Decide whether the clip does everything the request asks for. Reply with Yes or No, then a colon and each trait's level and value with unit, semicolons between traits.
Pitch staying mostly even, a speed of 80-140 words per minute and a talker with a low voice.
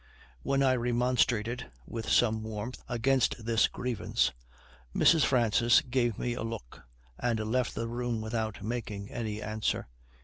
Yes: narrow, 2.0 semitones; slow, 135 wpm; low, 115 Hz